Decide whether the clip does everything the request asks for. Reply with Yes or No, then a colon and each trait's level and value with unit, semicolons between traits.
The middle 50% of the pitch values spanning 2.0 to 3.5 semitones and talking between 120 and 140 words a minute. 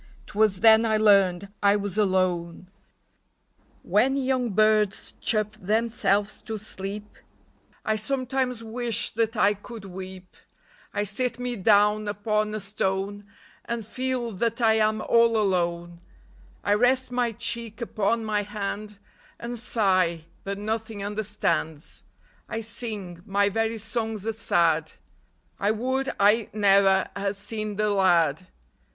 Yes: narrow, 2.4 semitones; slow, 135 wpm